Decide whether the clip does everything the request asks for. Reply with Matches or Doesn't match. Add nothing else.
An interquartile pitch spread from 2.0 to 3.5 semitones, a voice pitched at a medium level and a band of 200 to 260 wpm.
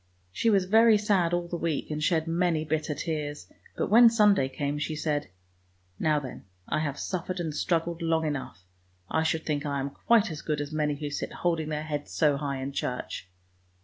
Matches